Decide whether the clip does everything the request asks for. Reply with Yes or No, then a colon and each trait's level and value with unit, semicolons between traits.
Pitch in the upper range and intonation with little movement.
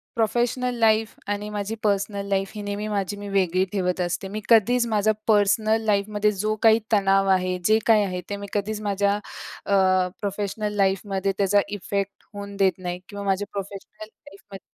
Yes: high, 205 Hz; narrow, 1.5 semitones